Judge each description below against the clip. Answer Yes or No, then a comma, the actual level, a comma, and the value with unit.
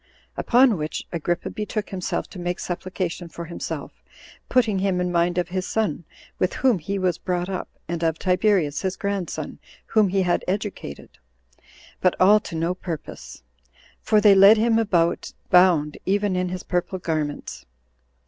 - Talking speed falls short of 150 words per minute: No, average, 160 wpm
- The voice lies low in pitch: No, medium, 185 Hz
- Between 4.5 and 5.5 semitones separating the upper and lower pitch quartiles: No, narrow, 2.6 semitones